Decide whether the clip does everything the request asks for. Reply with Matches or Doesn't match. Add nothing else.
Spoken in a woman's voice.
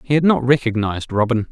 Doesn't match